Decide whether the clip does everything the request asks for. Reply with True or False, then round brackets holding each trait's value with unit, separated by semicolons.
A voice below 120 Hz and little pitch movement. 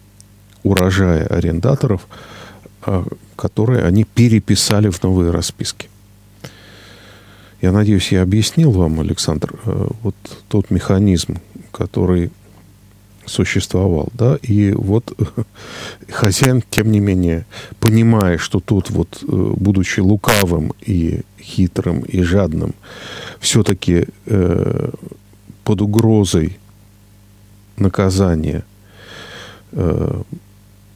True (100 Hz; 2.1 semitones)